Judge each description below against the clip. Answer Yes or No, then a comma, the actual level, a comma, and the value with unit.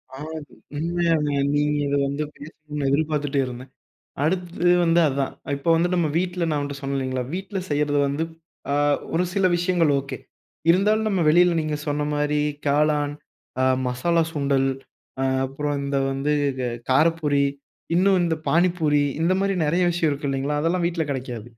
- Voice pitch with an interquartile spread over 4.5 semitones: No, average, 3.3 semitones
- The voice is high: No, medium, 150 Hz